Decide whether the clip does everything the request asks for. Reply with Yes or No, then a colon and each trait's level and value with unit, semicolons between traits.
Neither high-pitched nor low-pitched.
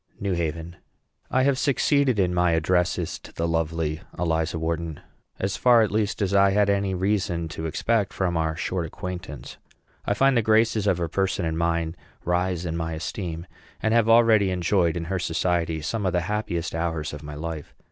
No: very low, 90 Hz